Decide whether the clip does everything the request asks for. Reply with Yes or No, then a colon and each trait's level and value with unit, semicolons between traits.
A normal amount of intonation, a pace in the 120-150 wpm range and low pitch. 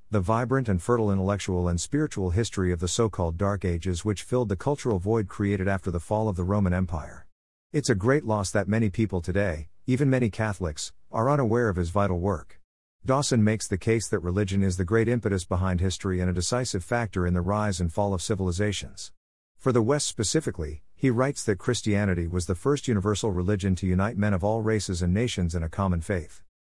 No: average, 3.7 semitones; fast, 205 wpm; low, 100 Hz